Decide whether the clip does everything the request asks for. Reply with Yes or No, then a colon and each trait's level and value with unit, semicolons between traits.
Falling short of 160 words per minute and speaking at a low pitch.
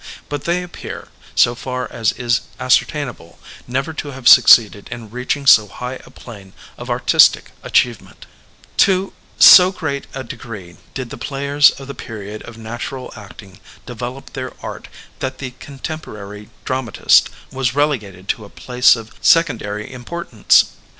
Yes: average, 150 wpm; low, 125 Hz